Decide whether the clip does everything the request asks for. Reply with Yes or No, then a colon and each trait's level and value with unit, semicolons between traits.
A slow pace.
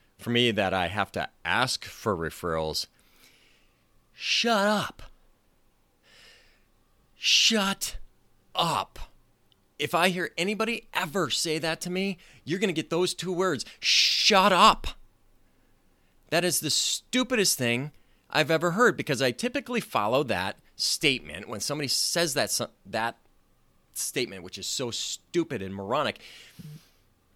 Yes: slow, 125 wpm